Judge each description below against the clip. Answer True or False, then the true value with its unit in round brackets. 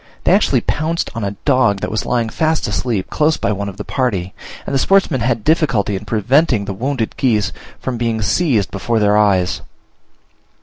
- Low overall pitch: True (115 Hz)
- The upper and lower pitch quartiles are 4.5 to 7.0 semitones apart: True (4.9 semitones)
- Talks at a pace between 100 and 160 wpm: False (185 wpm)